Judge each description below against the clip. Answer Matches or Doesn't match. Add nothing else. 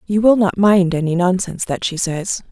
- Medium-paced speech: Doesn't match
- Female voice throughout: Matches